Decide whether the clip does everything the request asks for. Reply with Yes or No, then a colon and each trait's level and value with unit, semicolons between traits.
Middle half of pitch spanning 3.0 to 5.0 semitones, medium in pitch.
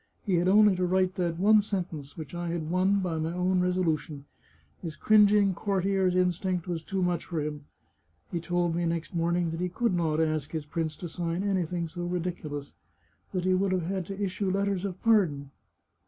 No: narrow, 2.4 semitones; medium, 180 Hz